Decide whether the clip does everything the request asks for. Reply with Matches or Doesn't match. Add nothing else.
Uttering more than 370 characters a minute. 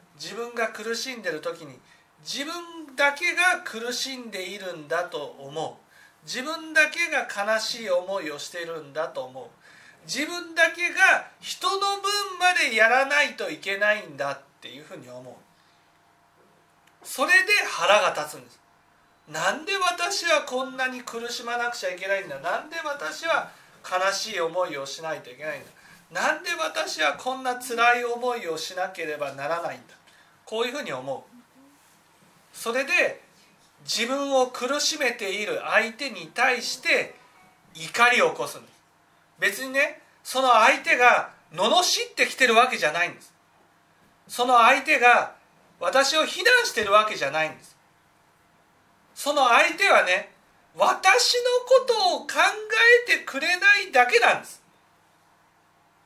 Doesn't match